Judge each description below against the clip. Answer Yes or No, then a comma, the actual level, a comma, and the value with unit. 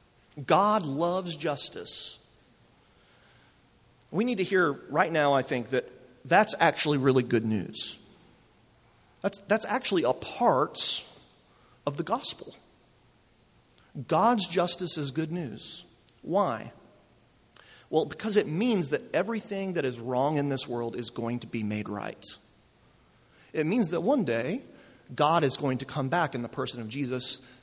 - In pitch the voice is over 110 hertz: Yes, medium, 140 Hz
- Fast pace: No, average, 140 wpm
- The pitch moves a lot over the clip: Yes, wide, 5.7 semitones